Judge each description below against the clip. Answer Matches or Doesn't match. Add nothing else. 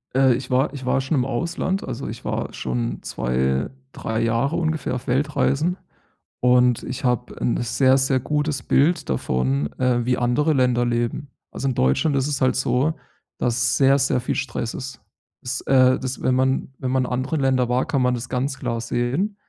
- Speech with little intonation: Matches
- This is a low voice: Matches